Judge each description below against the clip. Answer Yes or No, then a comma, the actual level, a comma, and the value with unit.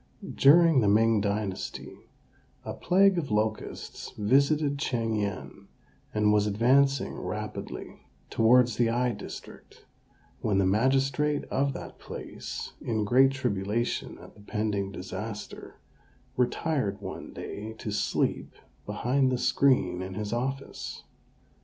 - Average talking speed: No, slow, 120 wpm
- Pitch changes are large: No, average, 4.5 semitones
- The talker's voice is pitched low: Yes, low, 115 Hz